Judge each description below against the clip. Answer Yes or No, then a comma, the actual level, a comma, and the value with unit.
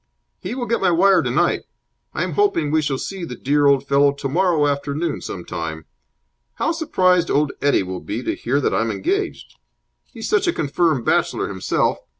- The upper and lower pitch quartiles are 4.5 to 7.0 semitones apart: Yes, average, 5.1 semitones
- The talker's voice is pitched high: No, medium, 150 Hz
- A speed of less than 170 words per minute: No, average, 175 wpm